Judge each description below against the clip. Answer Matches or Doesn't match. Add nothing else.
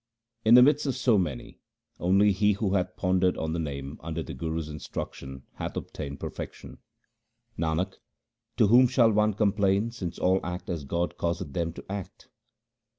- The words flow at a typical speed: Matches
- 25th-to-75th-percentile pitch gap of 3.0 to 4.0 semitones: Doesn't match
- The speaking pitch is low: Matches